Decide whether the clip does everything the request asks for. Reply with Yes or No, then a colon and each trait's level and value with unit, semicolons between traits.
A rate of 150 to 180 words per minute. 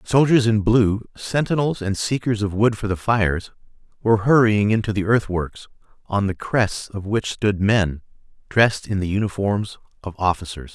Yes: average, 160 wpm